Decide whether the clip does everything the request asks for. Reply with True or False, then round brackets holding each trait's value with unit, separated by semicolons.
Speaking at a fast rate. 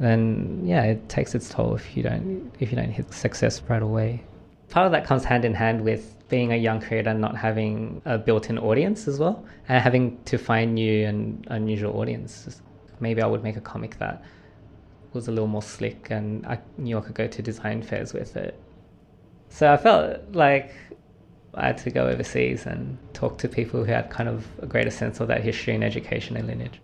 True (210 wpm)